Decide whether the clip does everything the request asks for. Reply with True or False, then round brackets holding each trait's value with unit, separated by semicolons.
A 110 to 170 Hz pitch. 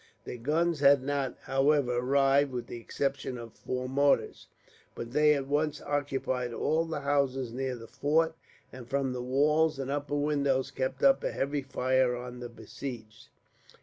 True (135 Hz)